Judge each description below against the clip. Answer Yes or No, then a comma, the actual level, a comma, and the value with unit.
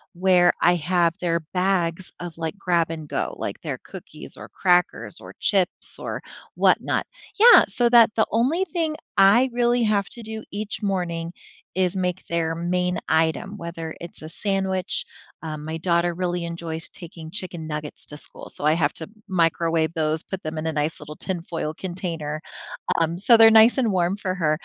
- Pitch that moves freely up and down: No, average, 3.2 semitones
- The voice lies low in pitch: No, medium, 175 Hz